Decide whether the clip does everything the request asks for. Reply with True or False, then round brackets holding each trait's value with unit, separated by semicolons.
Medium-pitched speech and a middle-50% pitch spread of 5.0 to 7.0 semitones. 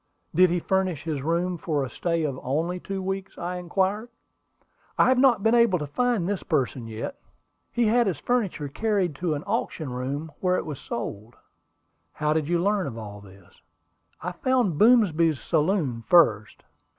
True (175 Hz; 5.4 semitones)